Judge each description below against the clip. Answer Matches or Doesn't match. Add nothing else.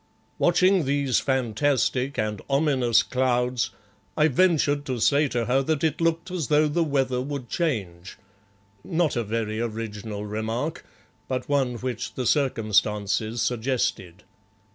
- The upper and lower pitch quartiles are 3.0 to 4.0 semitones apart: Doesn't match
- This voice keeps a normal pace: Doesn't match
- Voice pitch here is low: Matches